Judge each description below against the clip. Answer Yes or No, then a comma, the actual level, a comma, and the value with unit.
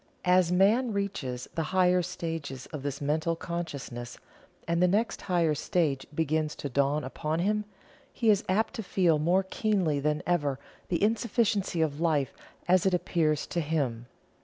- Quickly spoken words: No, average, 160 wpm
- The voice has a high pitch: No, medium, 170 Hz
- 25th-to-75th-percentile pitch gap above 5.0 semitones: No, average, 4.0 semitones